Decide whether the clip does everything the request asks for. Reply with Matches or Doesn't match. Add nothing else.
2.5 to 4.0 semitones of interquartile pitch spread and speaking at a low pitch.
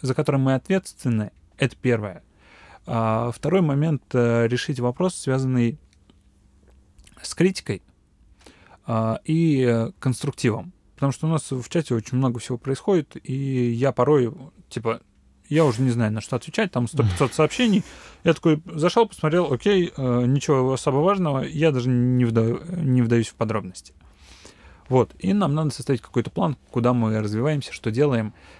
Doesn't match